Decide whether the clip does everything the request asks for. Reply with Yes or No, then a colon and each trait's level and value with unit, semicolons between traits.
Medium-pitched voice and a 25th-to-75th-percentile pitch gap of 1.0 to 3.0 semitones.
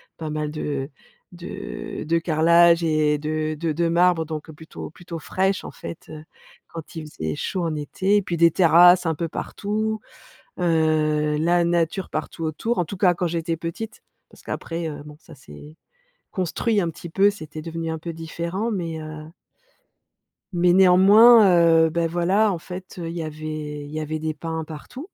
Yes: medium, 165 Hz; narrow, 2.4 semitones